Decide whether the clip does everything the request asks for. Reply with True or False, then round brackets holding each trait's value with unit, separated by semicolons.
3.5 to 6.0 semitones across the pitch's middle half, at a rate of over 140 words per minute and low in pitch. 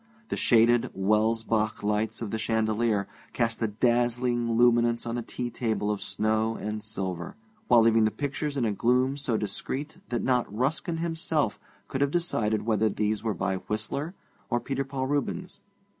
False (2.8 semitones; 165 wpm; 115 Hz)